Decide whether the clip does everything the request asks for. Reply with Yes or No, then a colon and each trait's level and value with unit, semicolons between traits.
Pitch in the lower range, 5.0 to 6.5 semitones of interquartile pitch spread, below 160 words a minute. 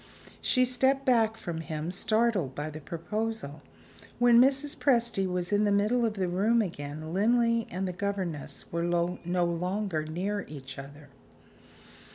No: high, 190 Hz; wide, 5.6 semitones; average, 150 wpm